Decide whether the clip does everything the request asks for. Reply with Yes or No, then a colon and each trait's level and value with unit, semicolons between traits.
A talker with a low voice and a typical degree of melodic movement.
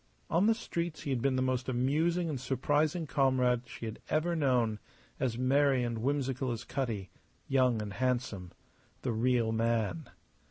Yes: low, 130 Hz; average, 3.3 semitones